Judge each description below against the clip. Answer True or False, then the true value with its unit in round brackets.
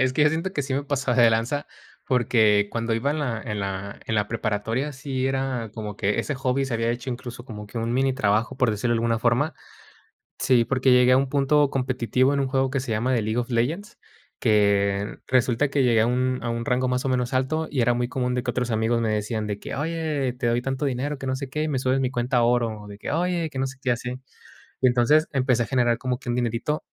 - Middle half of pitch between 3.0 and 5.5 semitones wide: False (2.6 semitones)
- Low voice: True (125 Hz)